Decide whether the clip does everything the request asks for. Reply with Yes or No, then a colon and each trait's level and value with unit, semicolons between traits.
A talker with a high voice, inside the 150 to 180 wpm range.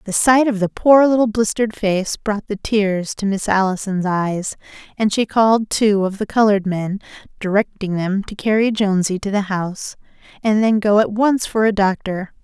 No: high, 205 Hz; average, 190 wpm